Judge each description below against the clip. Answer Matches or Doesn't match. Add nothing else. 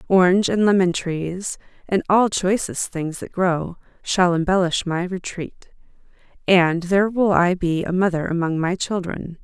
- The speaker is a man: Doesn't match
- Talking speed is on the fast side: Doesn't match